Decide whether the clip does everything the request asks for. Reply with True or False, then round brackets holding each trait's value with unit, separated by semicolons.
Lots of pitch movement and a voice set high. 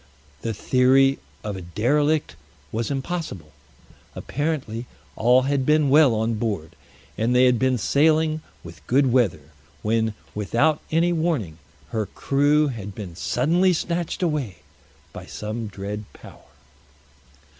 False (5.9 semitones; 125 Hz)